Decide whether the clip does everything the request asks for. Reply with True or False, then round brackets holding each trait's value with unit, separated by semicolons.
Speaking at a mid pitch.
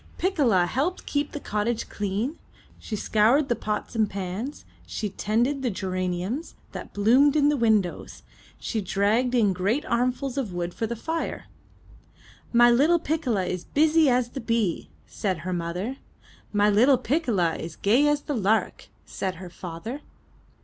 False (225 Hz)